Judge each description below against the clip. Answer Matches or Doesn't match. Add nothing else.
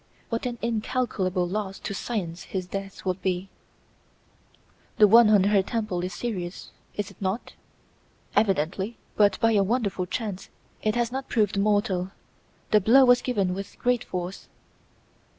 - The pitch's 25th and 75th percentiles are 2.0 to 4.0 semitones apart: Matches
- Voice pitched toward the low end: Doesn't match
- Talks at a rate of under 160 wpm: Matches